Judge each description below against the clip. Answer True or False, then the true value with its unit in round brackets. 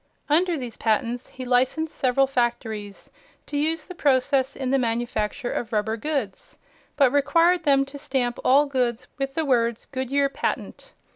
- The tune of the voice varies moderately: True (3.1 semitones)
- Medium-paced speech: True (155 wpm)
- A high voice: True (260 Hz)